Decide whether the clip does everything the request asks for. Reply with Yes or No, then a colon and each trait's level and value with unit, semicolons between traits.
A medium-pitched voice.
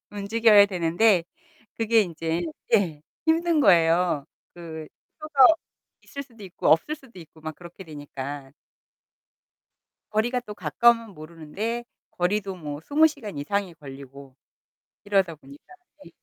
Yes: medium, 180 Hz